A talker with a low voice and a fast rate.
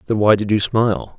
Yes: low, 105 Hz; fast, 255 wpm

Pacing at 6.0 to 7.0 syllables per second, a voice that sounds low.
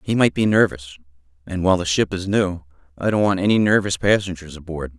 Yes: 6.1 syllables/s; very low, 90 Hz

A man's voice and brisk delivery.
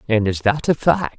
Yes: male; fast, 255 wpm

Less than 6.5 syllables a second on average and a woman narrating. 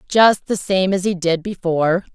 Yes: 4.7 syllables/s; female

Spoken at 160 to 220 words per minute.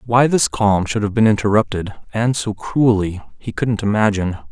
Yes: average, 175 wpm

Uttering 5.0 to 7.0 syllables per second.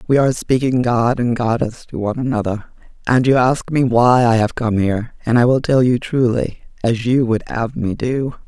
Yes: 5.1 syllables/s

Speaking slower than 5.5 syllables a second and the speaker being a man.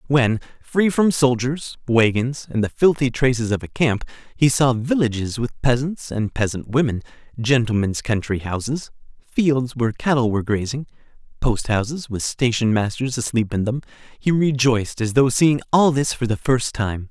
Yes: 4.8 syllables/s; male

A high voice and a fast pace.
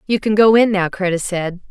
Yes: high, 195 Hz; fast, 245 wpm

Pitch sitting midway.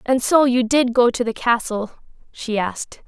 No: high, 240 Hz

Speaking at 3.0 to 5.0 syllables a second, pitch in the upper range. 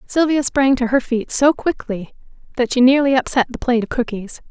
No: 5.4 syllables/s; very high, 255 Hz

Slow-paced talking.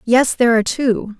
No: average, 200 wpm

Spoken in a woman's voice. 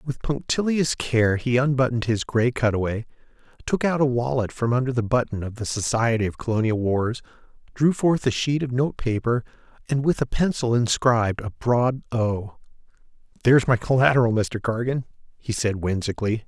No: male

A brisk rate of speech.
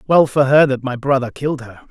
Yes: fast, 250 wpm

